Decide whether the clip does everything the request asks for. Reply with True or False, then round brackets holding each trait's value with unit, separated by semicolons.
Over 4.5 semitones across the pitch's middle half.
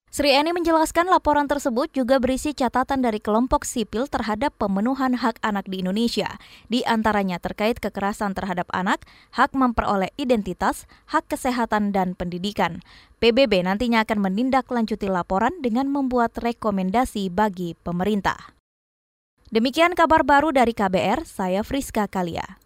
True (5.0 semitones)